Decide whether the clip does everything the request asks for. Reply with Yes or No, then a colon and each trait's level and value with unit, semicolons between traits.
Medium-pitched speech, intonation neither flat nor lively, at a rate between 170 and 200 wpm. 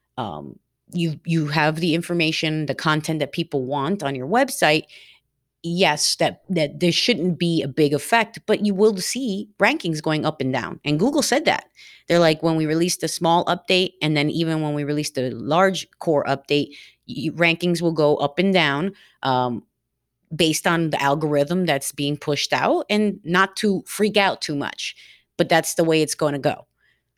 Yes: medium, 160 Hz; average, 3.6 semitones; average, 190 wpm